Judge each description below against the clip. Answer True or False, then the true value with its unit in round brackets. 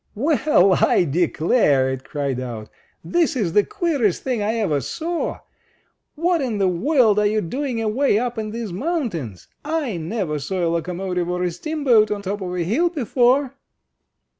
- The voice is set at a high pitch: True (210 Hz)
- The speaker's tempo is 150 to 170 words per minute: True (165 wpm)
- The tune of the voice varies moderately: False (7.4 semitones)